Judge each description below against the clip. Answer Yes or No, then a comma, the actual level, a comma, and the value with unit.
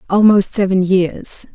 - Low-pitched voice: No, high, 195 Hz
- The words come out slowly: Yes, slow, 115 wpm